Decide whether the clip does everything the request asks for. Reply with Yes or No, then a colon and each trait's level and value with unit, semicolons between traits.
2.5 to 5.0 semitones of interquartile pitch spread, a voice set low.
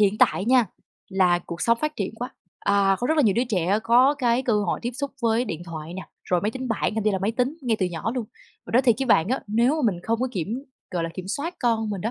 No: average, 4.6 semitones; high, 225 Hz